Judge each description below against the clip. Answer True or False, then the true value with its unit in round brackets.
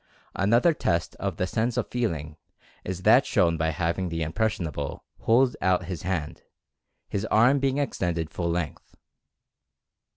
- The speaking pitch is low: True (90 Hz)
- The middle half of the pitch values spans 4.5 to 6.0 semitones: True (5.2 semitones)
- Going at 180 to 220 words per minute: False (140 wpm)